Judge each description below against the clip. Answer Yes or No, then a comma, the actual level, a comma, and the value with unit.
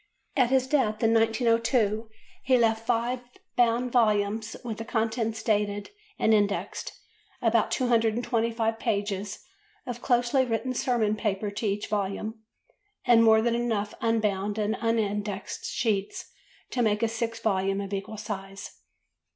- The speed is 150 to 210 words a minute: No, slow, 135 wpm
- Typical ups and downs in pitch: No, narrow, 2.1 semitones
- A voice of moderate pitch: No, high, 225 Hz